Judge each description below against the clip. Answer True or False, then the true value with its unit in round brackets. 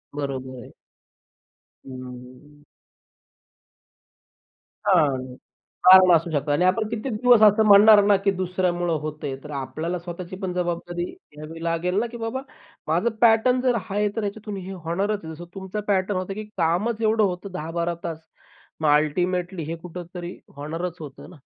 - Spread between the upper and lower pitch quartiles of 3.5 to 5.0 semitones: True (4.1 semitones)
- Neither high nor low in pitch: True (180 Hz)